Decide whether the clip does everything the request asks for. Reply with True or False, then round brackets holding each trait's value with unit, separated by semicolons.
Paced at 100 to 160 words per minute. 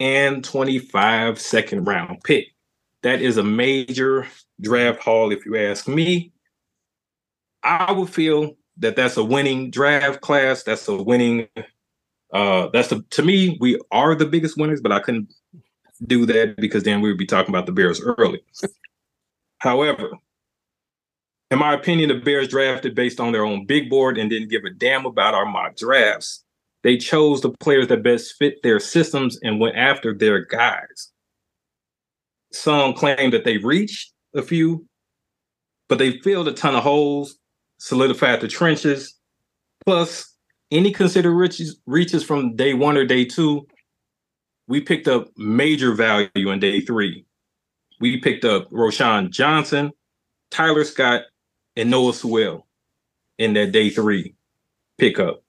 True (150 wpm)